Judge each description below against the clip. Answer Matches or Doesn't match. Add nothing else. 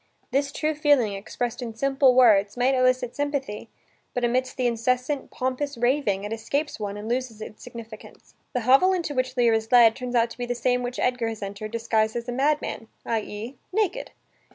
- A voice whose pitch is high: Matches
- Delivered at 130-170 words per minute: Doesn't match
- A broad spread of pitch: Doesn't match